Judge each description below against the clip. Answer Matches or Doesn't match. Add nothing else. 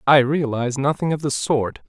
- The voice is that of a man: Matches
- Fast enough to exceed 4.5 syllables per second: Matches